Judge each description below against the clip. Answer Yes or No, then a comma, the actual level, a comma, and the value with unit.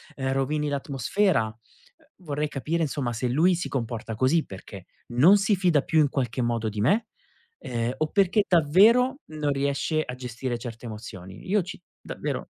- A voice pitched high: No, medium, 140 Hz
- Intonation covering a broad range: Yes, wide, 6.5 semitones